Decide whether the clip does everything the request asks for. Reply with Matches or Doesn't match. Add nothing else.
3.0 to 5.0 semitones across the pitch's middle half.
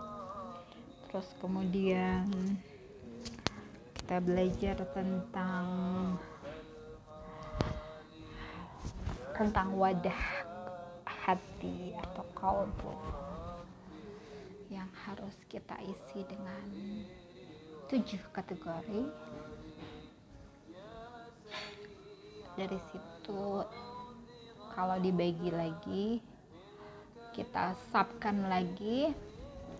Doesn't match